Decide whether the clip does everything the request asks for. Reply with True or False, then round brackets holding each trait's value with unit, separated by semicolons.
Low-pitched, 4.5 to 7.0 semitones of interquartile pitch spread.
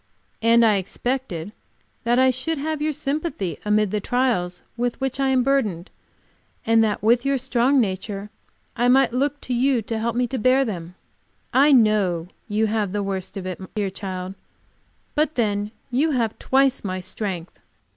False (230 Hz; 4.9 semitones)